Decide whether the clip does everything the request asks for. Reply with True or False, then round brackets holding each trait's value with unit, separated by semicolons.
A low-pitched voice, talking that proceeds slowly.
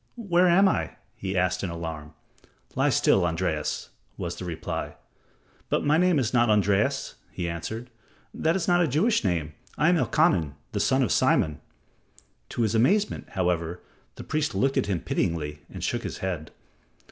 False (105 Hz; 170 wpm)